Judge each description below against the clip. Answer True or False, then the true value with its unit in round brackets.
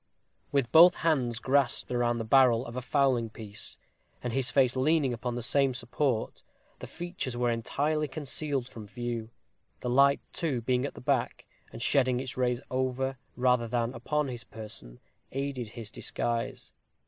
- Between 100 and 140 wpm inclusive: False (160 wpm)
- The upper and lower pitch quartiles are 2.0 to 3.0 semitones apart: True (2.6 semitones)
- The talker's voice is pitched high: False (125 Hz)